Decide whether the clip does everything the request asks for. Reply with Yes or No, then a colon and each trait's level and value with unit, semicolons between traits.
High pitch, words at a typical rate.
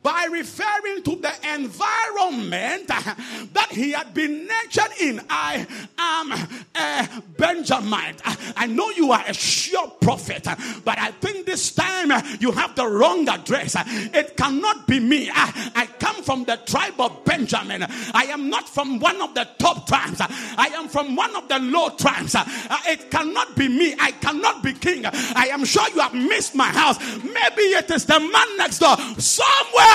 Yes: very high, 300 Hz; average, 170 wpm